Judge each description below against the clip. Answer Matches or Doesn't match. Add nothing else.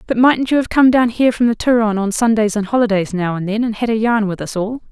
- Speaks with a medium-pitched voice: Doesn't match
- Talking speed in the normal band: Doesn't match